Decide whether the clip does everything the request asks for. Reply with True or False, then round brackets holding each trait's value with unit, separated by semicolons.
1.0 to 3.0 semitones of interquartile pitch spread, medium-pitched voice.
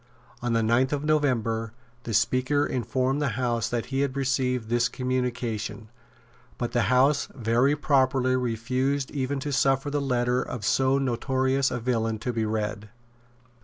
False (2.6 semitones; 125 Hz)